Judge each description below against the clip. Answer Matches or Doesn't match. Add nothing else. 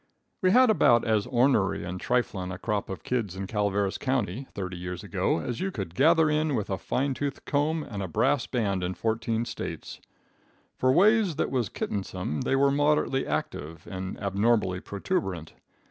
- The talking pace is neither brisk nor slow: Matches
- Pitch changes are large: Matches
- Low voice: Matches